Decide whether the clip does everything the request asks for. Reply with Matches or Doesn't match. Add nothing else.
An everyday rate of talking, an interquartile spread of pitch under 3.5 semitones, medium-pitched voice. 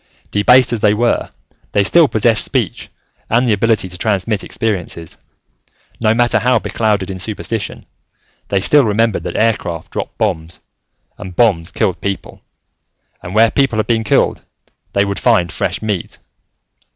Doesn't match